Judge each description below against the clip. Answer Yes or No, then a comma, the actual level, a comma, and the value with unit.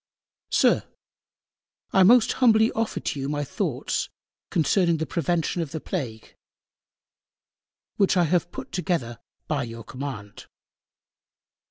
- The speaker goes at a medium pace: No, slow, 120 wpm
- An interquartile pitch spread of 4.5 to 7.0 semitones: Yes, average, 5.3 semitones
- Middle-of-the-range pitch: Yes, medium, 165 Hz